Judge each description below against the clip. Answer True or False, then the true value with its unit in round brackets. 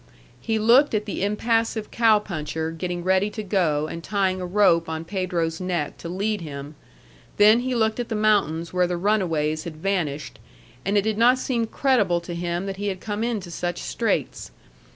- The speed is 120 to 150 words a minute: False (190 wpm)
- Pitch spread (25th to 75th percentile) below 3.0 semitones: False (4.1 semitones)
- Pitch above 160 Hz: True (190 Hz)